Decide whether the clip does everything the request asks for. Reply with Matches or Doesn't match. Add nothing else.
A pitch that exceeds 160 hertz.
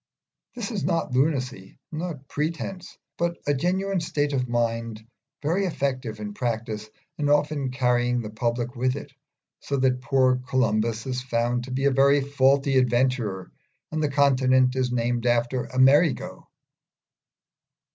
Doesn't match